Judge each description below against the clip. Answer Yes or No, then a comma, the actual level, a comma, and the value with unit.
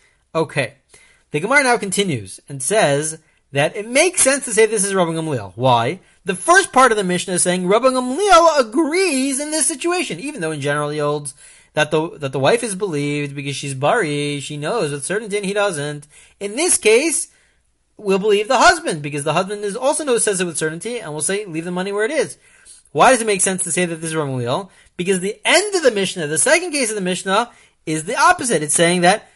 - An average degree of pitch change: No, wide, 8.5 semitones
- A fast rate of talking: Yes, fast, 225 wpm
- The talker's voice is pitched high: Yes, high, 195 Hz